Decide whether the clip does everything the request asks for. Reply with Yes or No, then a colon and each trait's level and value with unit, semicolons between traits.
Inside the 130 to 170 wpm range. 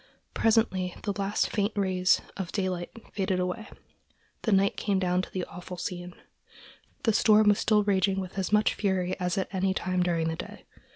No: average, 180 wpm